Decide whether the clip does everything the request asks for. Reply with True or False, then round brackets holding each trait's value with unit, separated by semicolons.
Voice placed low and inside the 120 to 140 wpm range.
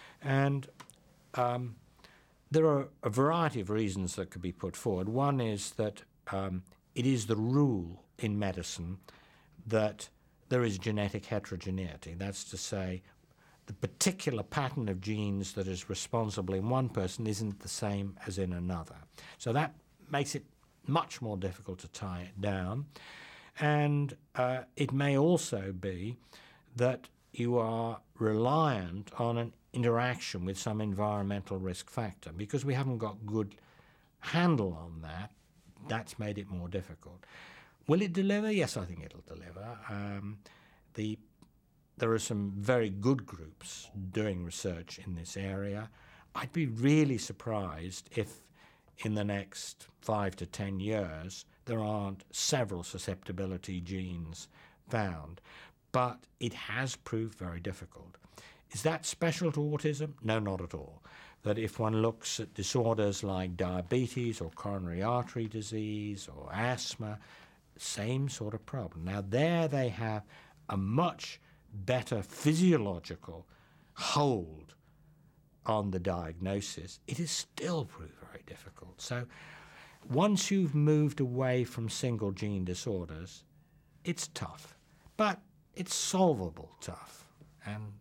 True (110 Hz; 135 wpm)